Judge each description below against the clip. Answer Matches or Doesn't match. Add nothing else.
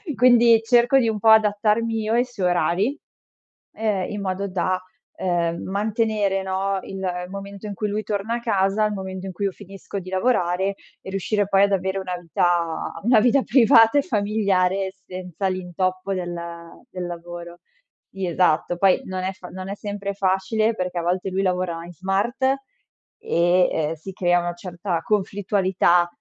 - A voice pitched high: Matches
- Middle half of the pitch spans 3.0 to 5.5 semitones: Doesn't match